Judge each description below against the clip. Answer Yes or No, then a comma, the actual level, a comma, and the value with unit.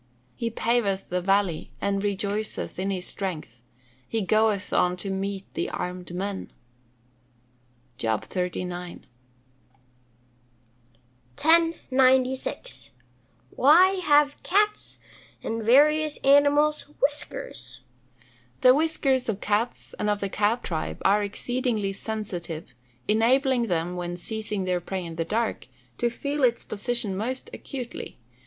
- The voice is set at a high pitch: Yes, high, 215 Hz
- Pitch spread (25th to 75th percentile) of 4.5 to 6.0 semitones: Yes, wide, 5.6 semitones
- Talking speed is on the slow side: Yes, slow, 115 wpm